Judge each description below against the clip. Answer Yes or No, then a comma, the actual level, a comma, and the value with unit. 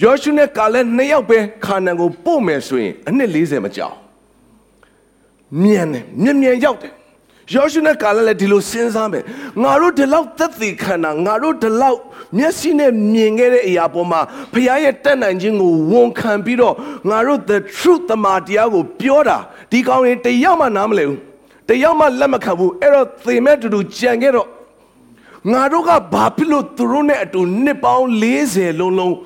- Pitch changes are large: Yes, wide, 5.8 semitones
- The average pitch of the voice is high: Yes, high, 245 Hz